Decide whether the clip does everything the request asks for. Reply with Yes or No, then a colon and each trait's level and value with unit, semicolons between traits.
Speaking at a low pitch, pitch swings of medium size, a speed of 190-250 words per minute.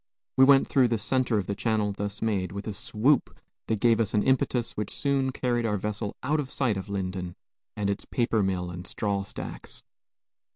Yes: low, 105 Hz; average, 3.8 semitones; average, 200 wpm